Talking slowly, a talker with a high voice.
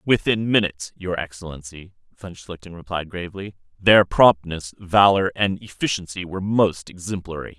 No: slow, 125 wpm; very low, 90 Hz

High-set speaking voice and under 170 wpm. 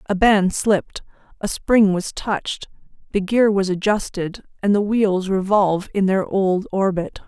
Yes: high, 195 Hz; average, 155 wpm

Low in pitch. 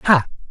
No: medium, 145 Hz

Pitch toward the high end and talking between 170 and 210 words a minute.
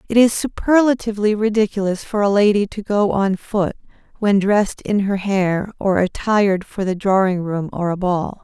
Yes: high, 200 Hz; average, 180 wpm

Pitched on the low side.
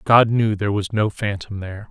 Yes: low, 105 Hz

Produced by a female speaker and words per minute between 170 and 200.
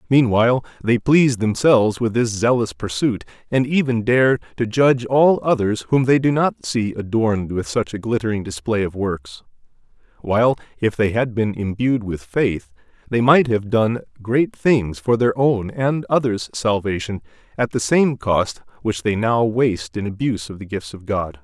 No: male; average, 175 wpm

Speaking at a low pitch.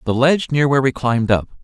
Yes: low, 130 Hz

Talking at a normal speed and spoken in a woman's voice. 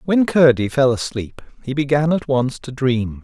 No: average, 185 wpm; male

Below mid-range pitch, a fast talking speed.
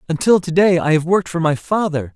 No: medium, 165 Hz; fast, 225 wpm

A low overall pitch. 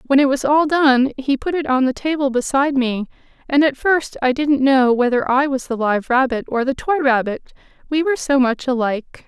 No: very high, 265 Hz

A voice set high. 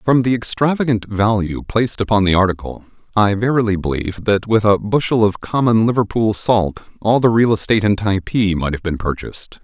No: low, 105 Hz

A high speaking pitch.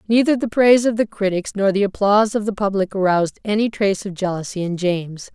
Yes: high, 200 Hz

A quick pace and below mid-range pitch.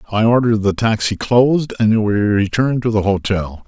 No: average, 180 wpm; low, 110 Hz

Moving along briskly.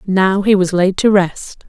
Yes: fast, 215 wpm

